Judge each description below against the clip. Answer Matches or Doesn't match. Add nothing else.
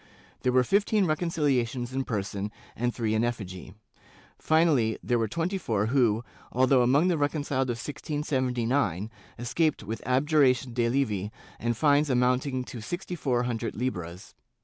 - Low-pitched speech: Matches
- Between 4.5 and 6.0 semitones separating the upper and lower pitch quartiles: Doesn't match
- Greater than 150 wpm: Doesn't match